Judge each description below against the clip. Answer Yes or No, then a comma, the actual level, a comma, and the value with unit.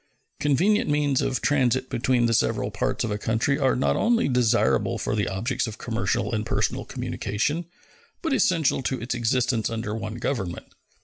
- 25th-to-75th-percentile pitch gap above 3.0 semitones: Yes, average, 4.2 semitones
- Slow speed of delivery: No, average, 170 wpm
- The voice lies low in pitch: Yes, low, 125 Hz